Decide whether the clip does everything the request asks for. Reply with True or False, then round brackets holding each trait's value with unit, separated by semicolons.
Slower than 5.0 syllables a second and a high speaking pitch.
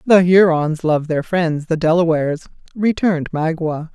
False (4.6 syllables/s; 165 Hz)